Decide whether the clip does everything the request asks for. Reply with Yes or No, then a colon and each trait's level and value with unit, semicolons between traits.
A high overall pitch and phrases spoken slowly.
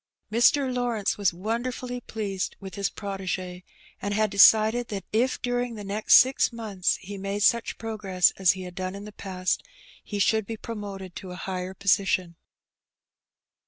No: high, 205 Hz; average, 165 wpm